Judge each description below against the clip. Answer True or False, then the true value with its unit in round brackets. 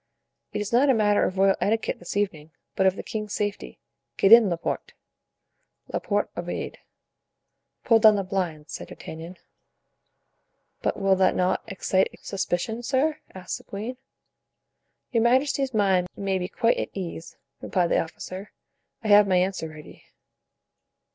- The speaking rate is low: False (150 wpm)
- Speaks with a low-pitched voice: False (195 Hz)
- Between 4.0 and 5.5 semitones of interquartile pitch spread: False (3.3 semitones)